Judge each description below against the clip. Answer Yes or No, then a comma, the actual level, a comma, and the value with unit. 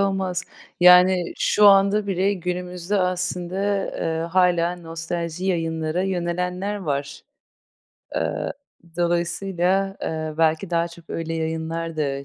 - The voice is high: No, medium, 175 Hz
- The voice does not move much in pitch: Yes, narrow, 2.2 semitones